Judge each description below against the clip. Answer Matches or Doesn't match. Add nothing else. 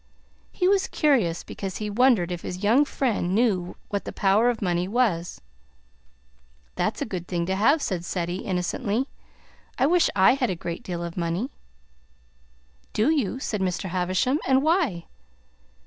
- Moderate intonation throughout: Doesn't match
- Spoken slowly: Doesn't match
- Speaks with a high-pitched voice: Matches